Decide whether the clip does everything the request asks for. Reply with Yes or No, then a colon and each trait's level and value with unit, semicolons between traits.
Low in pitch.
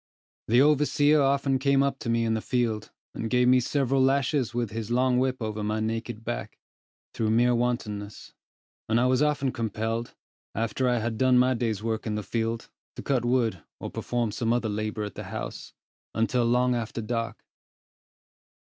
Yes: low, 120 Hz